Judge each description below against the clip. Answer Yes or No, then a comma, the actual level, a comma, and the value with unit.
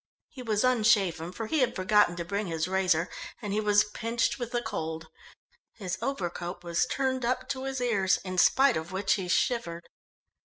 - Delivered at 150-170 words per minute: No, average, 180 wpm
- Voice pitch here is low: No, high, 205 Hz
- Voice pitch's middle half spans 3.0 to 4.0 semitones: No, average, 5.3 semitones